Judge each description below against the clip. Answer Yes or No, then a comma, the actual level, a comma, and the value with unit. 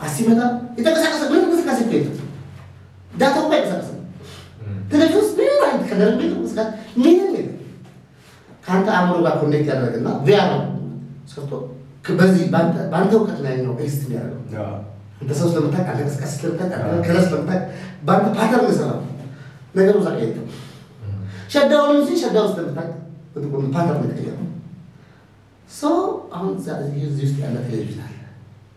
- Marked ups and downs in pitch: Yes, wide, 8.0 semitones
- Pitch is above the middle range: No, medium, 160 Hz